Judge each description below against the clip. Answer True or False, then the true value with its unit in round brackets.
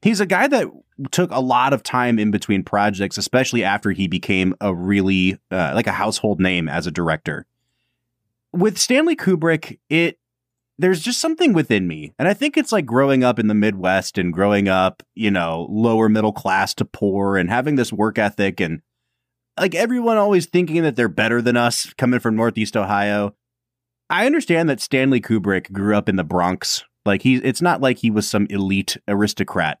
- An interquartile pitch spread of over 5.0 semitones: True (5.4 semitones)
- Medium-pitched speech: False (110 Hz)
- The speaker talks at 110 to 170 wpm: False (190 wpm)